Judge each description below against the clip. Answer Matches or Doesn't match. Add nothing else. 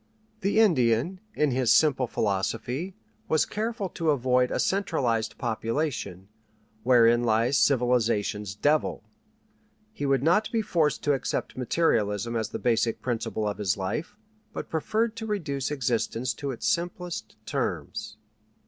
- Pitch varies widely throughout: Matches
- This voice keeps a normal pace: Doesn't match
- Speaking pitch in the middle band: Doesn't match